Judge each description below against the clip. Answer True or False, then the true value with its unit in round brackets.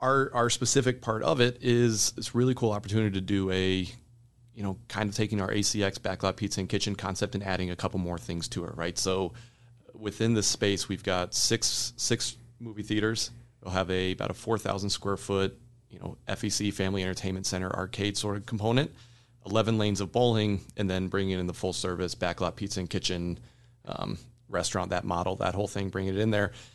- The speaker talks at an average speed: True (195 wpm)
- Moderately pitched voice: False (105 Hz)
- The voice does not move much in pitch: False (3.8 semitones)